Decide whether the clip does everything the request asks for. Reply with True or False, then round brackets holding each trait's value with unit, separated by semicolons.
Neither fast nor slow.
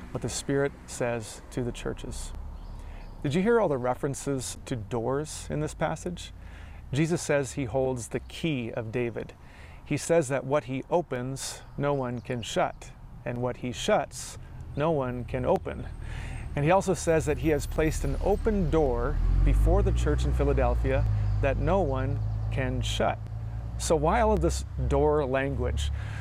True (165 wpm)